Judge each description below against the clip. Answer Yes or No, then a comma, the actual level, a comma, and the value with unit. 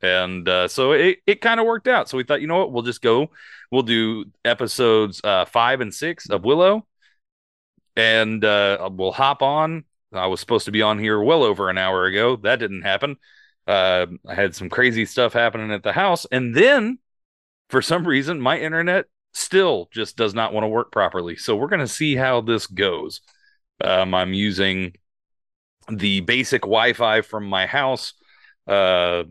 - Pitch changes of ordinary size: No, wide, 8.0 semitones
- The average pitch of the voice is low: Yes, low, 110 Hz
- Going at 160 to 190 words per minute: Yes, average, 185 wpm